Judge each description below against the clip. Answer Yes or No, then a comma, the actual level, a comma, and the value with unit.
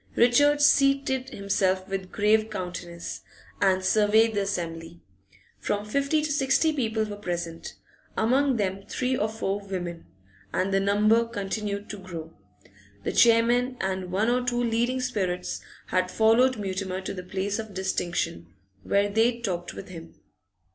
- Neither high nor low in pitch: No, high, 205 Hz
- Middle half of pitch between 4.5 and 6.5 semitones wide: No, average, 4.1 semitones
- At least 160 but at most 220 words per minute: No, average, 145 wpm